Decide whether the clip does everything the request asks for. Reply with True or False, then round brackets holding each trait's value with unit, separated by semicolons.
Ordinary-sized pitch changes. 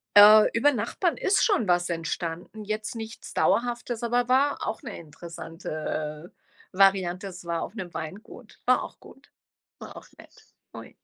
False (5.7 semitones)